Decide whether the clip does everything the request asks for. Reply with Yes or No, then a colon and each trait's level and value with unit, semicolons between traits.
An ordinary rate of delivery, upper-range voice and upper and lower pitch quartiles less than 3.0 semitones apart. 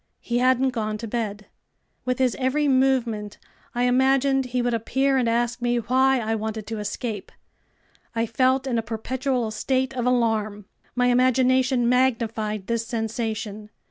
Yes: average, 150 wpm; high, 240 Hz; narrow, 2.6 semitones